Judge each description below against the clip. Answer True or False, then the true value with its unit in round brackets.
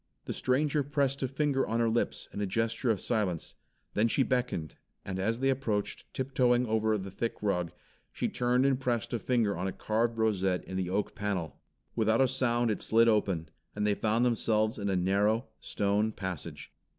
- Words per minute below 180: False (190 wpm)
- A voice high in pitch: False (110 Hz)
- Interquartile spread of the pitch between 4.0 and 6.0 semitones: False (3.6 semitones)